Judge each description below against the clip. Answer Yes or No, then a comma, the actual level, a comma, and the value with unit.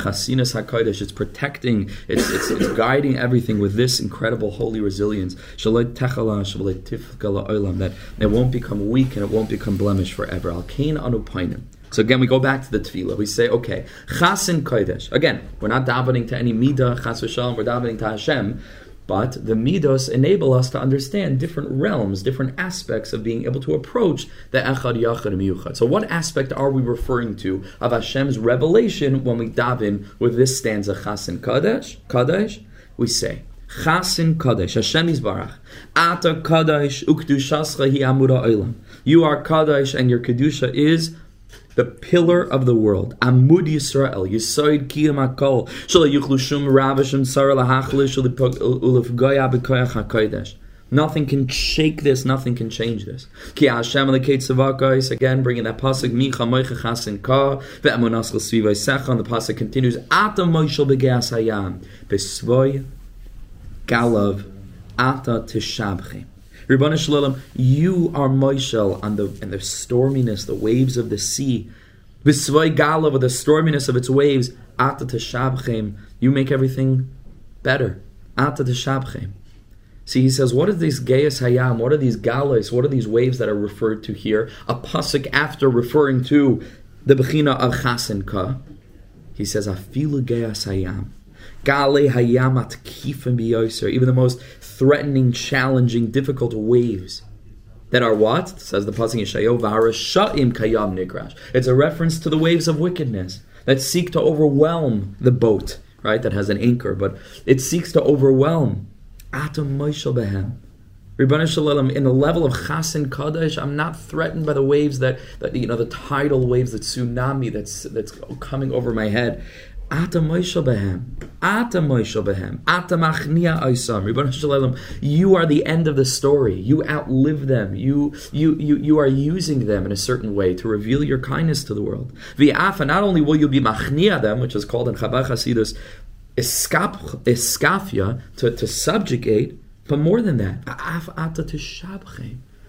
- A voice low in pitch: Yes, low, 125 Hz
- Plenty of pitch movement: No, average, 4.4 semitones